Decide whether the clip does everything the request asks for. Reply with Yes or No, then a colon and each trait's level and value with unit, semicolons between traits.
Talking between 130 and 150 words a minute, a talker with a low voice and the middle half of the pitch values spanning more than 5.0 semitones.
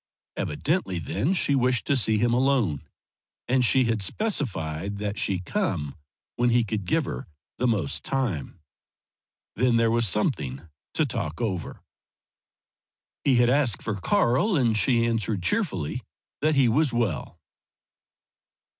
Yes: slow, 135 wpm; low, 115 Hz; wide, 5.4 semitones